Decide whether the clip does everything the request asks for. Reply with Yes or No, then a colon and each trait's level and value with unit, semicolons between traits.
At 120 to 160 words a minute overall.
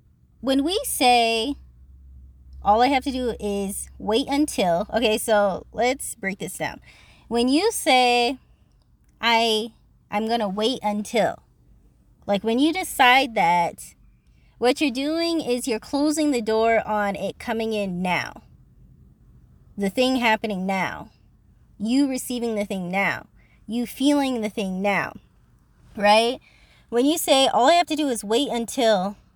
Yes: average, 145 wpm